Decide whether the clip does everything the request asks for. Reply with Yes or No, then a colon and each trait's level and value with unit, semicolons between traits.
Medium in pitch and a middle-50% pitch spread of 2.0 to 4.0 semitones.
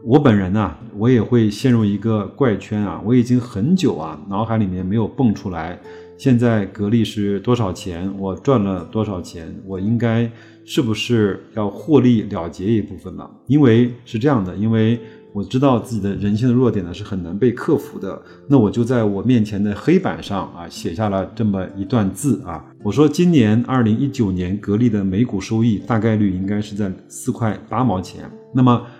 No: low, 110 Hz; average, 3.5 semitones